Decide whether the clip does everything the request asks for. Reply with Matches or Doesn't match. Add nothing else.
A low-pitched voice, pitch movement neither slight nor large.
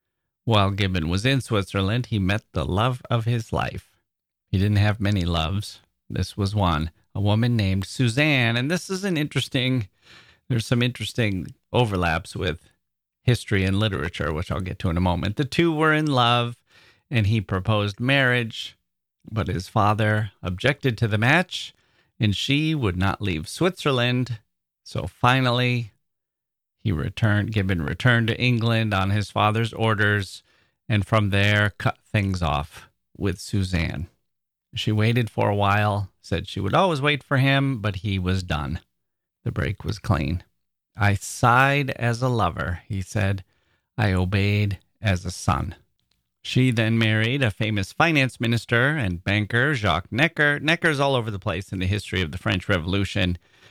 Matches